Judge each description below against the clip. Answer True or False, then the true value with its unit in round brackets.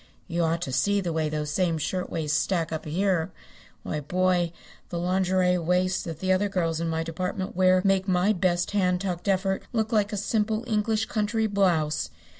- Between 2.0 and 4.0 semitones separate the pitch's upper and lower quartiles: True (2.9 semitones)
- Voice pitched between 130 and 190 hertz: True (185 Hz)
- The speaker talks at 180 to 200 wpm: True (185 wpm)